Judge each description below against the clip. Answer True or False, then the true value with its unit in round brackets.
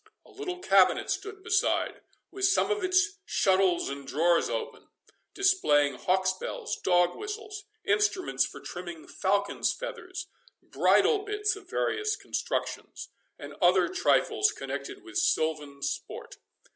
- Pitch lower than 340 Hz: False (370 Hz)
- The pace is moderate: False (125 wpm)